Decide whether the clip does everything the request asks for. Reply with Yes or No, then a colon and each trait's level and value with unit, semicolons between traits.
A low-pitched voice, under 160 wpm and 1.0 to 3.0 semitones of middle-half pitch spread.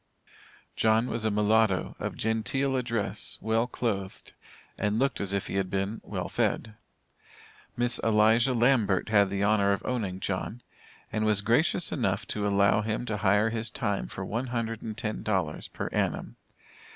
No: low, 110 Hz; average, 165 wpm; narrow, 2.5 semitones